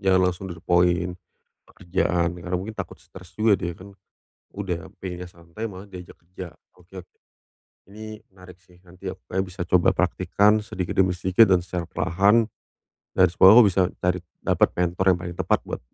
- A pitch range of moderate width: No, narrow, 1.6 semitones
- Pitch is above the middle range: No, very low, 90 Hz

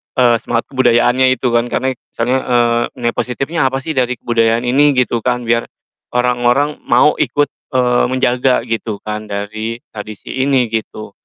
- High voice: No, low, 120 Hz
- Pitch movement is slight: Yes, narrow, 2.0 semitones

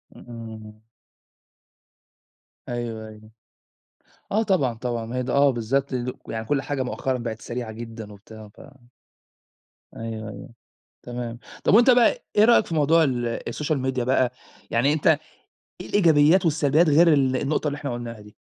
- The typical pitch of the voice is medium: No, low, 125 Hz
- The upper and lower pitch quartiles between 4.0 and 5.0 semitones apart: Yes, average, 4.4 semitones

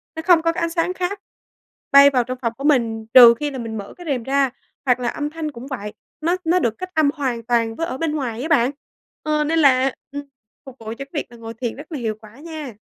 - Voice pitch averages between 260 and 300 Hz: Yes, very high, 275 Hz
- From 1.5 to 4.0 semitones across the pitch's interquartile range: No, average, 5.0 semitones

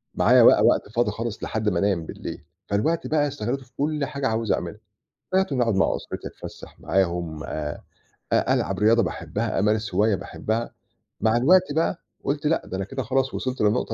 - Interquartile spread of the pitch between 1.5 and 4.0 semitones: No, average, 4.9 semitones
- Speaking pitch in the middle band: No, low, 115 Hz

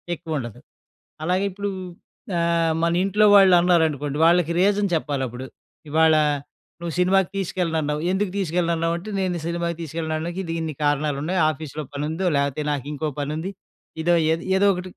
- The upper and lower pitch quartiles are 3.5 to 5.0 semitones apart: No, average, 3.0 semitones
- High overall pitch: No, medium, 165 Hz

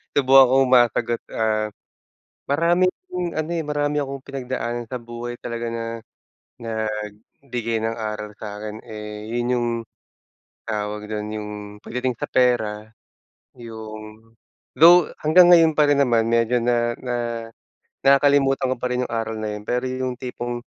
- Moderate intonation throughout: Yes, average, 3.4 semitones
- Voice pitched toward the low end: Yes, low, 120 Hz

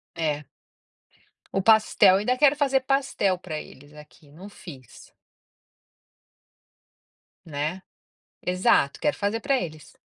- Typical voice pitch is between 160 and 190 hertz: Yes, medium, 185 Hz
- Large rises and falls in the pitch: Yes, wide, 6.9 semitones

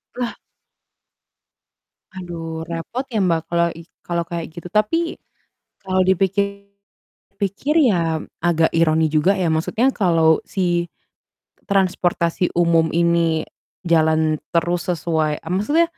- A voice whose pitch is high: No, medium, 170 Hz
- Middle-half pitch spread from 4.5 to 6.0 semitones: No, average, 2.9 semitones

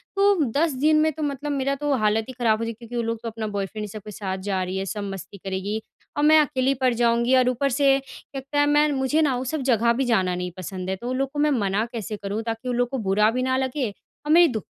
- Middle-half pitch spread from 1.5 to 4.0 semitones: No, average, 4.7 semitones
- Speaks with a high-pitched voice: Yes, high, 245 Hz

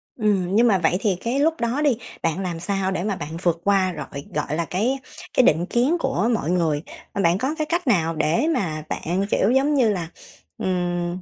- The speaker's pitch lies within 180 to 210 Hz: Yes, high, 190 Hz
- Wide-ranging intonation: Yes, wide, 5.8 semitones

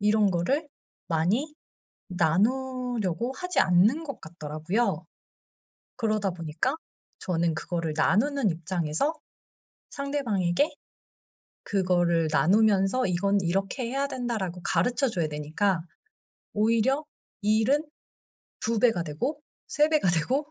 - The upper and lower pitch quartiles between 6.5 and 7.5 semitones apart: Yes, wide, 6.8 semitones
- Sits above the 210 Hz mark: No, high, 205 Hz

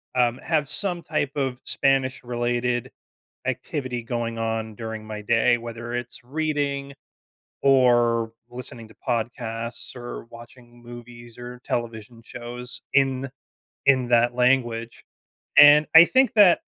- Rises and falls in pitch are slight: Yes, narrow, 2.2 semitones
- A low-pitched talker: Yes, low, 120 Hz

